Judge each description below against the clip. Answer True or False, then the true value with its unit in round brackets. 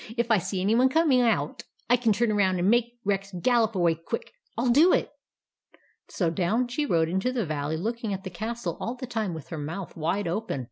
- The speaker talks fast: True (235 wpm)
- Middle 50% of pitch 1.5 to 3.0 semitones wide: False (5.4 semitones)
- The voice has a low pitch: False (210 Hz)